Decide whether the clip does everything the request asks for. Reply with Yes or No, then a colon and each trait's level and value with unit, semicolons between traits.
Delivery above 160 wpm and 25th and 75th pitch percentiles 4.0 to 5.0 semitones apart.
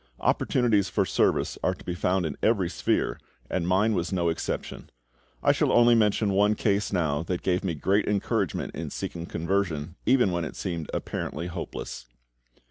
No: average, 170 wpm; average, 3.4 semitones